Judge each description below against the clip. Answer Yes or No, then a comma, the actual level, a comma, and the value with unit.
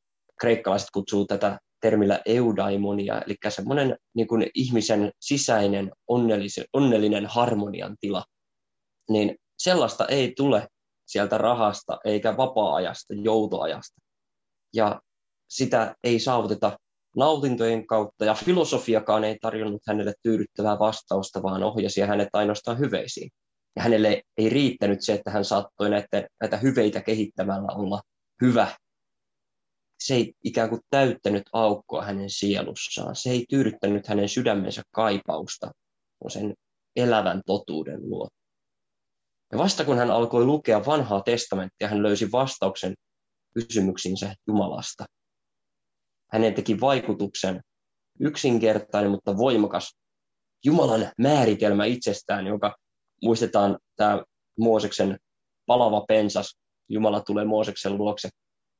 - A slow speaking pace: No, average, 105 wpm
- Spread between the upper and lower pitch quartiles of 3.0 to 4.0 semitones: No, narrow, 2.4 semitones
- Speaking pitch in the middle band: No, low, 105 Hz